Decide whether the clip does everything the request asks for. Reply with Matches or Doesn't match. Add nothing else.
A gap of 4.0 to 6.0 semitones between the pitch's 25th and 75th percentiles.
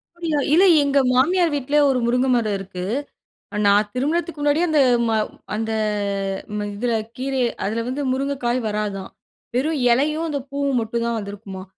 Matches